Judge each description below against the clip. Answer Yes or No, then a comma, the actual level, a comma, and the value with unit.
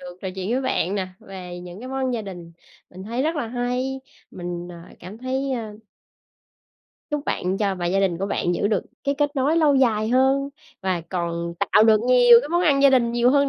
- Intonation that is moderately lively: No, wide, 6.3 semitones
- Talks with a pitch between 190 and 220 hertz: No, high, 230 Hz